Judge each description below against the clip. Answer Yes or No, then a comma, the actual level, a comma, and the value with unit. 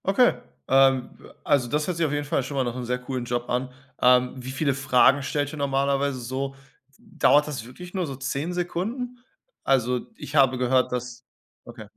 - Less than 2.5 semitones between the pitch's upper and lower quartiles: No, average, 2.8 semitones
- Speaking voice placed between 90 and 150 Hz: Yes, low, 135 Hz